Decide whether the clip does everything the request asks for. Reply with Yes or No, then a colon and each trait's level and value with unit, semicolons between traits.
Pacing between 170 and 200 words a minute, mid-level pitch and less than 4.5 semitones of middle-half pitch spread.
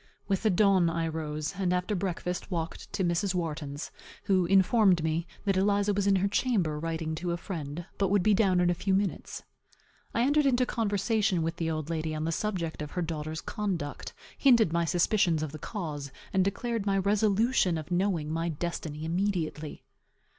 Yes: average, 185 wpm; medium, 180 Hz; average, 3.8 semitones